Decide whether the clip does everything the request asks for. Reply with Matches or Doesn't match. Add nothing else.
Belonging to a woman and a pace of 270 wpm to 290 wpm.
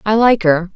Doesn't match